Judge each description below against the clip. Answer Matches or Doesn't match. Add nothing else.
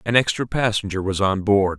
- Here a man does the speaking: Matches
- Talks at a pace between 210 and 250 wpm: Doesn't match